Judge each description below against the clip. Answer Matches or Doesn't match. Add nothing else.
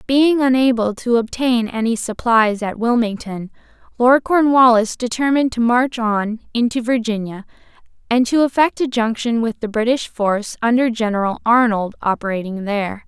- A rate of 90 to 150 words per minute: Matches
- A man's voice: Doesn't match